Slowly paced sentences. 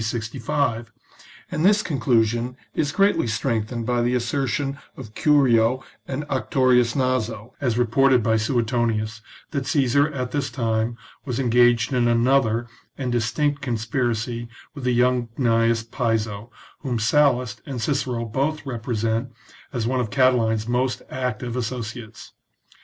Yes: slow, 130 wpm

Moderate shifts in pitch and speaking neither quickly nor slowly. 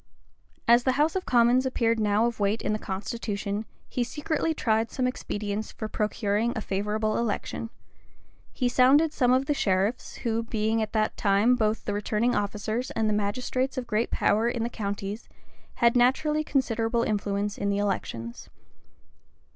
Yes: average, 3.0 semitones; average, 155 wpm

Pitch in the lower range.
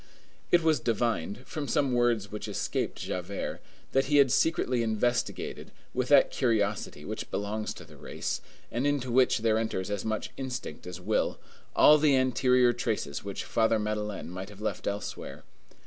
Yes: low, 115 Hz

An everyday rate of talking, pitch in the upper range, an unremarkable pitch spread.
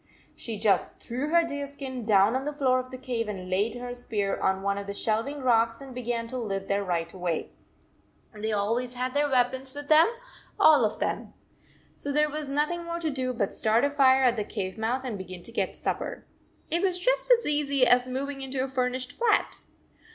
No: fast, 215 wpm; very high, 250 Hz; average, 4.6 semitones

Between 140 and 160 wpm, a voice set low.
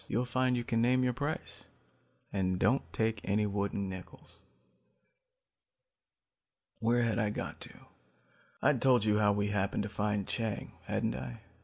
Yes: average, 150 wpm; low, 105 Hz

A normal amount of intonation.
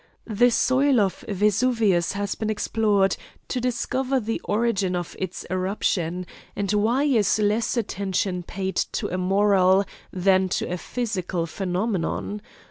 Yes: average, 3.3 semitones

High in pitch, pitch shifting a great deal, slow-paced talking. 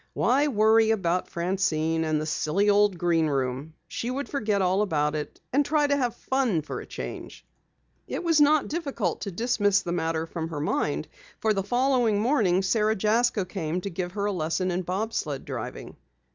No: high, 195 Hz; wide, 6.0 semitones; average, 185 wpm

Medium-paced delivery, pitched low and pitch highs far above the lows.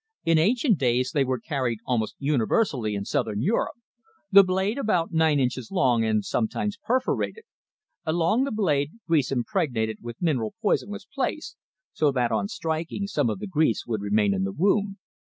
No: average, 170 wpm; medium, 145 Hz; wide, 8.7 semitones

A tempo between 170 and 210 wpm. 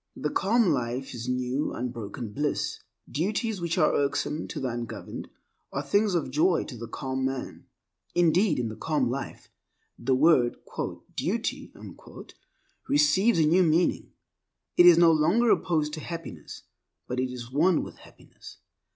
No: average, 150 wpm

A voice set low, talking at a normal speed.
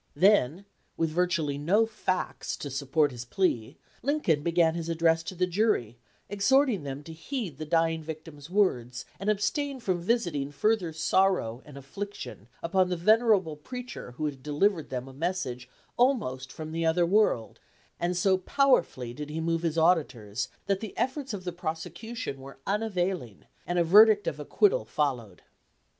No: medium, 170 Hz; average, 160 wpm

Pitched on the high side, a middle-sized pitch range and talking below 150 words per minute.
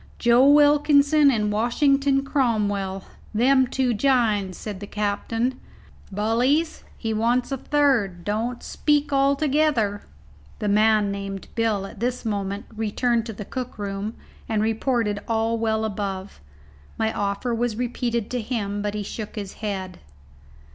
Yes: high, 225 Hz; average, 3.8 semitones; average, 140 wpm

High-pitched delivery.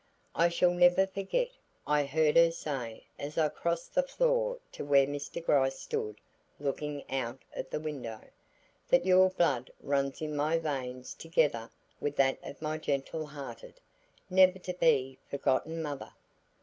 No: medium, 150 Hz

